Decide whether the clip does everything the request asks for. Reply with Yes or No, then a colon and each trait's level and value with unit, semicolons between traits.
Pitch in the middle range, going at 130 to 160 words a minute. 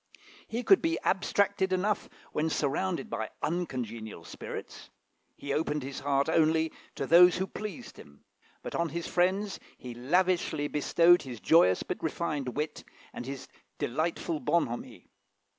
Yes: medium, 160 Hz; average, 140 wpm